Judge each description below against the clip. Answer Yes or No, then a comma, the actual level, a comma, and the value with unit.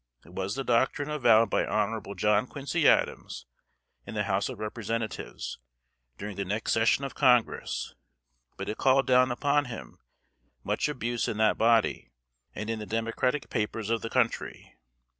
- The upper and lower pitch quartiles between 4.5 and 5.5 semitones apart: No, average, 3.1 semitones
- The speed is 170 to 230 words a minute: No, average, 160 wpm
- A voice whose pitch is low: Yes, low, 115 Hz